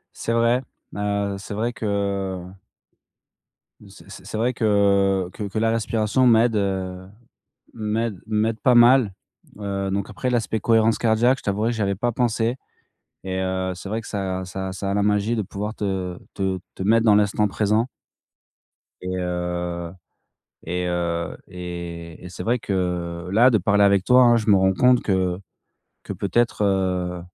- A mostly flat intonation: No, average, 3.2 semitones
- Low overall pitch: Yes, low, 100 Hz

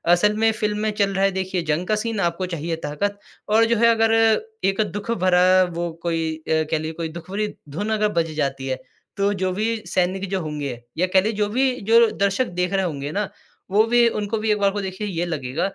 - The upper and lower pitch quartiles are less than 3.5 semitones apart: No, average, 4.0 semitones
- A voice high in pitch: Yes, high, 195 Hz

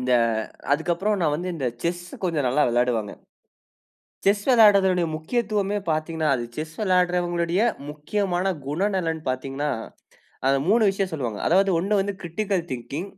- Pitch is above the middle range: No, medium, 175 Hz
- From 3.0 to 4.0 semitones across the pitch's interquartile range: No, average, 4.8 semitones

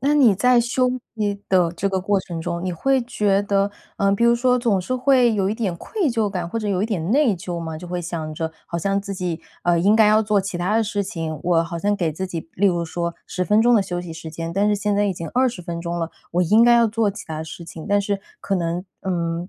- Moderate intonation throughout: Yes, average, 4.1 semitones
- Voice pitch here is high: Yes, high, 195 Hz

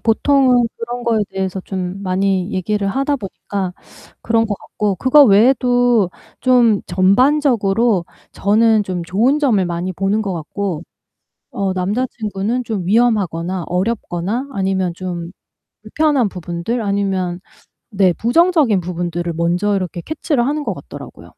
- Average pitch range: Yes, average, 4.6 semitones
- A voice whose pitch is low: No, high, 200 Hz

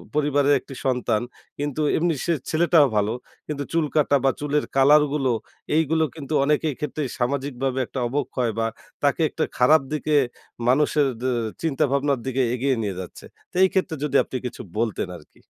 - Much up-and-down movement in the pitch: No, average, 2.9 semitones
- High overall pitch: No, medium, 140 Hz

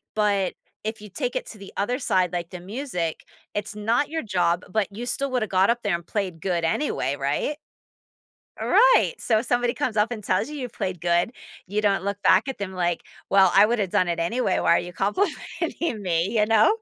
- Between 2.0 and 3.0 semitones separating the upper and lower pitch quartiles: No, average, 4.7 semitones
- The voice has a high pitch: Yes, high, 205 Hz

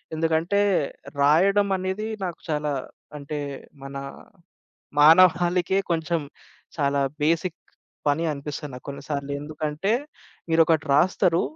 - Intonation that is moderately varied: Yes, average, 3.3 semitones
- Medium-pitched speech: Yes, medium, 160 Hz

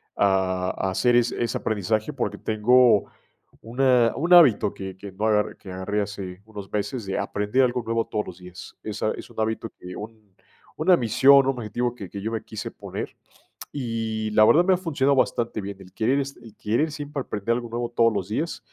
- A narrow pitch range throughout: No, average, 3.4 semitones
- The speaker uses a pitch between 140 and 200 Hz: No, low, 110 Hz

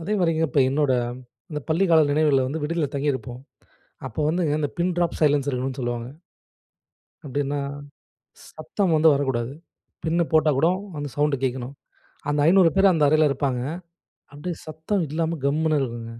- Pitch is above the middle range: No, medium, 150 Hz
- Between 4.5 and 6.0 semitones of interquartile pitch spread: No, average, 3.0 semitones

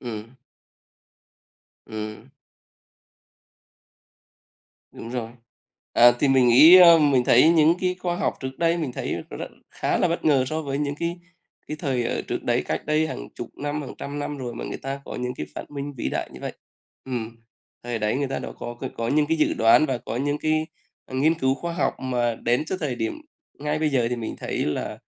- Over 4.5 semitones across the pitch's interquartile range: No, average, 4.2 semitones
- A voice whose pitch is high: No, low, 135 Hz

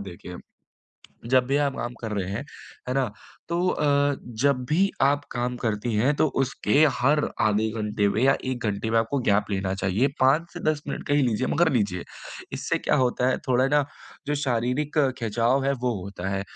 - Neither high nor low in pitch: No, low, 125 Hz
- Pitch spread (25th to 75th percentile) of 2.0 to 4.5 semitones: No, average, 4.9 semitones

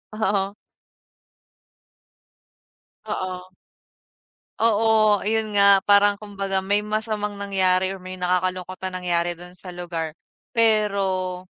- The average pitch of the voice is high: Yes, high, 195 Hz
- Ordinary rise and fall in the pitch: No, narrow, 2.3 semitones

